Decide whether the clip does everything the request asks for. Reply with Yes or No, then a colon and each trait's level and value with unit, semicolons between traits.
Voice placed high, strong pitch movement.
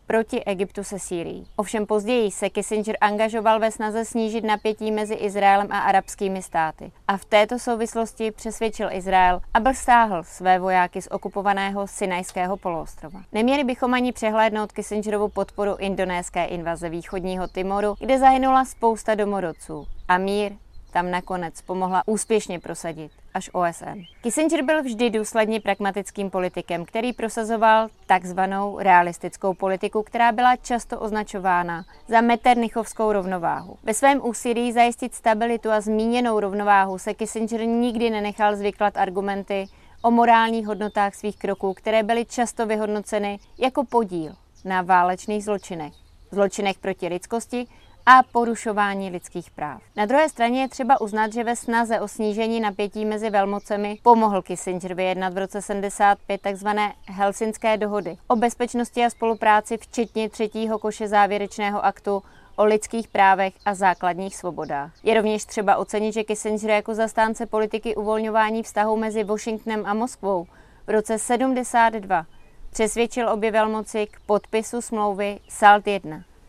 No: high, 210 Hz; narrow, 2.5 semitones